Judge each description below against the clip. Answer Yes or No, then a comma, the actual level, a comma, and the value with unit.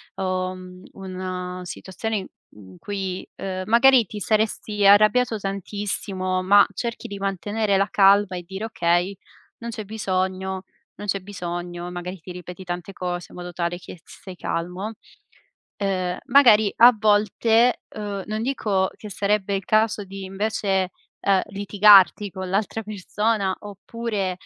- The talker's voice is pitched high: Yes, high, 195 Hz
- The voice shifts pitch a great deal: No, narrow, 2.3 semitones